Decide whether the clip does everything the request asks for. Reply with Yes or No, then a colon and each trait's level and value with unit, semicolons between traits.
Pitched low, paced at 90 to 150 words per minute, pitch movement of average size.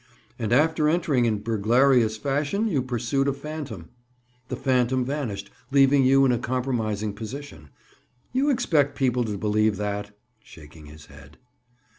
Yes: low, 125 Hz; average, 140 wpm; average, 4.9 semitones